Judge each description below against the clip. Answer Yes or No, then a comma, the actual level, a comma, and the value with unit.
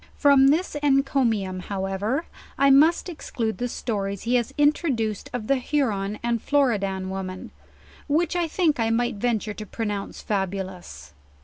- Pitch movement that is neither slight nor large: No, wide, 5.9 semitones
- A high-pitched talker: Yes, high, 230 Hz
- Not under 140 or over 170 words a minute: Yes, average, 150 wpm